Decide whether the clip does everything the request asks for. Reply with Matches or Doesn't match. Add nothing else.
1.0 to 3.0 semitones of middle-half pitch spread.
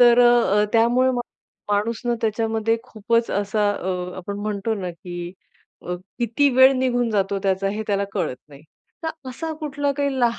Doesn't match